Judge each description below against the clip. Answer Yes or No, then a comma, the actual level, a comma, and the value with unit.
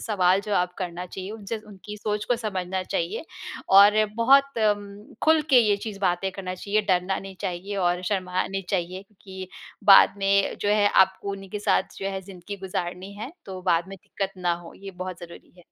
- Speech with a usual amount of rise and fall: No, narrow, 2.1 semitones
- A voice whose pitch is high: Yes, high, 195 Hz